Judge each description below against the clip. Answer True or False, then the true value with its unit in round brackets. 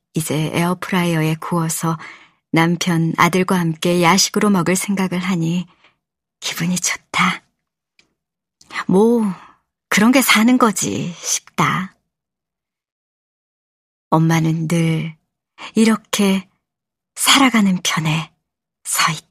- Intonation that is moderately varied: True (3.3 semitones)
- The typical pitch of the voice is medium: True (180 Hz)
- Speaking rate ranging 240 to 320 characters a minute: False (190 characters per minute)